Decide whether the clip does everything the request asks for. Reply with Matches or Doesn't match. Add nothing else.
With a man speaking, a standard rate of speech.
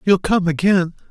Matches